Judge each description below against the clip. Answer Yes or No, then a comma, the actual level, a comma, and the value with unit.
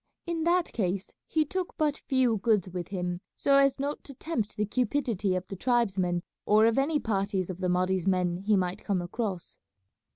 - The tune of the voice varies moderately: No, wide, 6.7 semitones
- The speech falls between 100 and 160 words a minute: No, average, 190 wpm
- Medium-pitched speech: No, high, 210 Hz